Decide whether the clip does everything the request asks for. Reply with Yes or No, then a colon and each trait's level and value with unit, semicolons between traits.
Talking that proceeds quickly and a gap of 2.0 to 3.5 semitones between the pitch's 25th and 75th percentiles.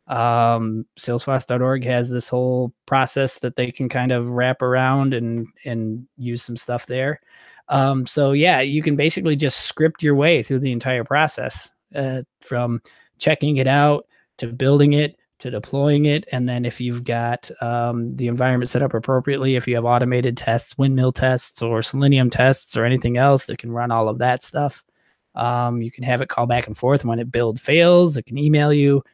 No: average, 190 wpm; narrow, 2.5 semitones